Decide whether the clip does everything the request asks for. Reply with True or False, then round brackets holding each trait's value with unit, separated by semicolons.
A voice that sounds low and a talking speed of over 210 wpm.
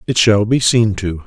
True (105 Hz; 235 wpm)